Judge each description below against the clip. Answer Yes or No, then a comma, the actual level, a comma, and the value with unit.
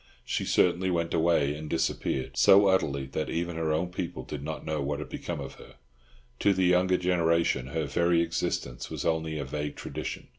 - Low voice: Yes, very low, 80 Hz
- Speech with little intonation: No, average, 3.0 semitones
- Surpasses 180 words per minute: Yes, average, 190 wpm